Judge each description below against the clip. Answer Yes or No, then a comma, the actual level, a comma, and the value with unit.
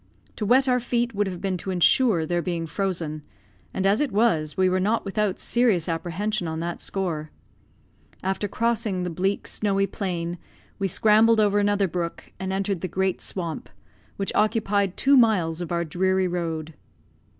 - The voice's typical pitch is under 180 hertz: No, high, 190 Hz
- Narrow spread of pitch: No, average, 3.4 semitones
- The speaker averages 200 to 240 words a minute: No, average, 170 wpm